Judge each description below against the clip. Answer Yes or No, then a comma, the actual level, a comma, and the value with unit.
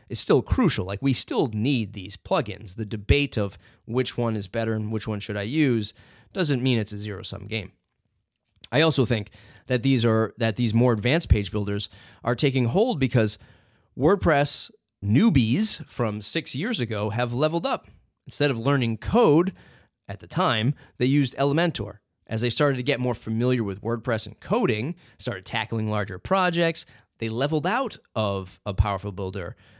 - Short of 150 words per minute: No, average, 175 wpm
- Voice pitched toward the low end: Yes, low, 115 Hz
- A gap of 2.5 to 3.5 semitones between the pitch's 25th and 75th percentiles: No, average, 4.4 semitones